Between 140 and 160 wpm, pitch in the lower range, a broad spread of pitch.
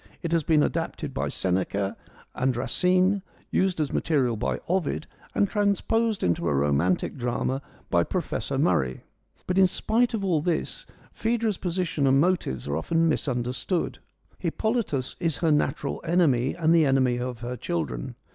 No: average, 155 wpm; medium, 155 Hz; wide, 7.0 semitones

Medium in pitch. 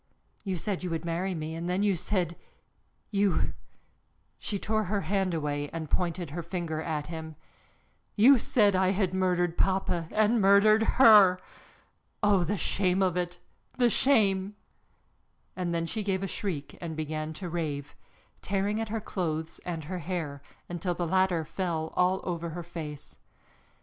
Yes: medium, 180 Hz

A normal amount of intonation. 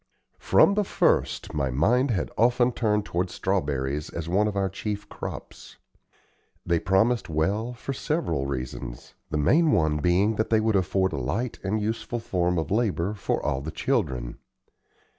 No: wide, 6.3 semitones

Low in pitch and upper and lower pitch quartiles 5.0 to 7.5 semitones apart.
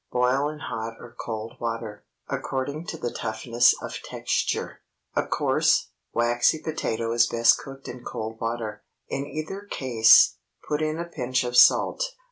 No: low, 120 Hz; average, 4.3 semitones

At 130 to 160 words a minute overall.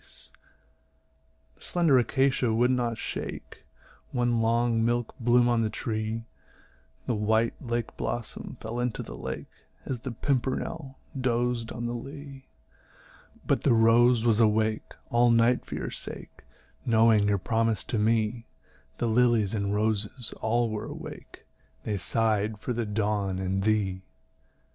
Yes: average, 140 wpm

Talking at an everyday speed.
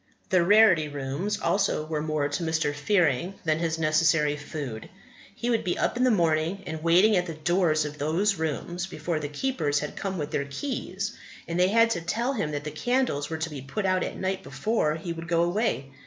No: fast, 215 wpm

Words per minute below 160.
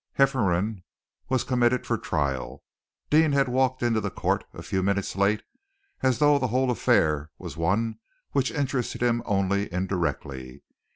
Yes: average, 150 wpm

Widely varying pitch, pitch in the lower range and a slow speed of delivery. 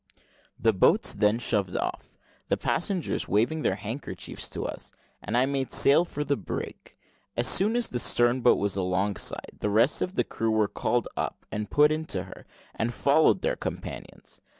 No: wide, 6.0 semitones; low, 120 Hz; average, 175 wpm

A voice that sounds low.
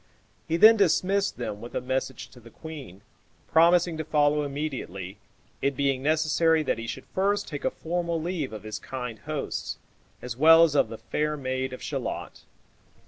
No: medium, 145 Hz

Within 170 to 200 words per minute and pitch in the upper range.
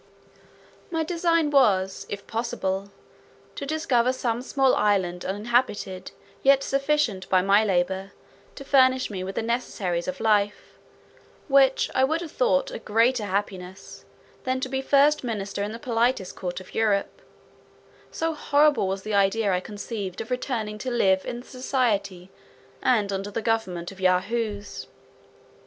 No: average, 145 wpm; high, 225 Hz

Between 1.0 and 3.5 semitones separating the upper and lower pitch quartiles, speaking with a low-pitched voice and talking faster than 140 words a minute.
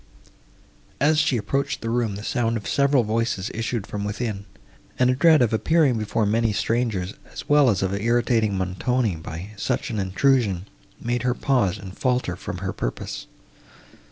No: average, 3.9 semitones; low, 115 Hz; average, 165 wpm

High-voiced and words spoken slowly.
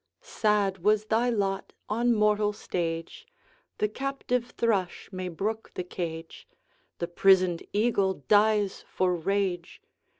Yes: high, 200 Hz; slow, 120 wpm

